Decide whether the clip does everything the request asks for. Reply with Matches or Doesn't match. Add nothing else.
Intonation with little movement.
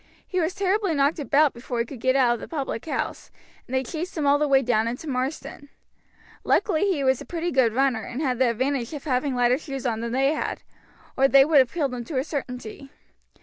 Doesn't match